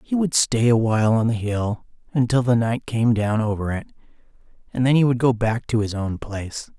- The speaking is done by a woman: No, male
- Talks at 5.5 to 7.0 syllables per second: No, 5.3 syllables/s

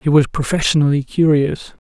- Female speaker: No, male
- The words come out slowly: Yes, slow, 130 wpm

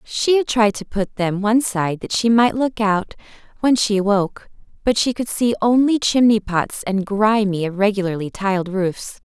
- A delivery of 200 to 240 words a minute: No, average, 180 wpm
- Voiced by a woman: Yes, female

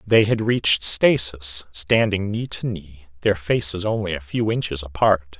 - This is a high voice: No, very low, 95 Hz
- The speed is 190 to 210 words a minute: No, average, 165 wpm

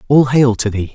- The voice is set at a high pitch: No, low, 125 Hz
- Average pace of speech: No, fast, 255 wpm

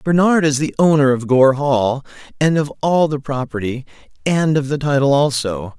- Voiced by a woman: No, male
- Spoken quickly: No, average, 175 wpm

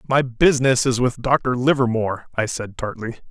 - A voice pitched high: No, low, 125 Hz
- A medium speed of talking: Yes, average, 165 wpm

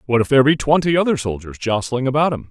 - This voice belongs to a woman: No, male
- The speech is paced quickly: Yes, fast, 240 wpm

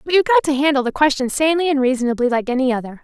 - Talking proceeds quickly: Yes, fast, 255 wpm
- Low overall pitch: No, very high, 280 Hz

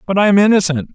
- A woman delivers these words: No, male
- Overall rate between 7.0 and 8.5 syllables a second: Yes, 7.6 syllables/s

